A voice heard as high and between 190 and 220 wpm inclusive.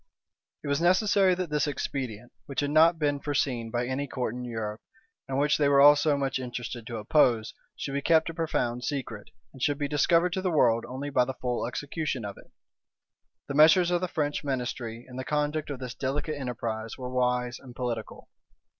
No: low, 135 Hz; average, 200 wpm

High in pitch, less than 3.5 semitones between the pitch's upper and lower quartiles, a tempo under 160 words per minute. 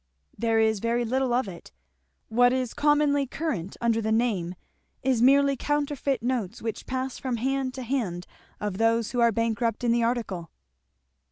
No: high, 235 Hz; average, 2.9 semitones; average, 165 wpm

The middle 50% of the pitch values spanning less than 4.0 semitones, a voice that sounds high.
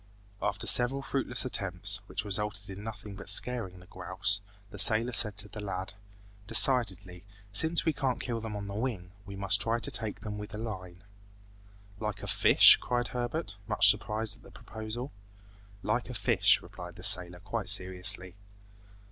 No: average, 3.2 semitones; low, 105 Hz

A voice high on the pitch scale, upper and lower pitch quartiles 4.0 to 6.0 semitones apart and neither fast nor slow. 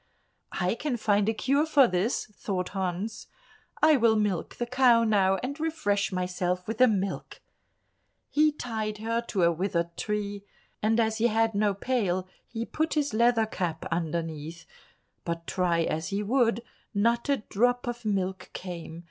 Yes: high, 210 Hz; average, 4.5 semitones; average, 160 wpm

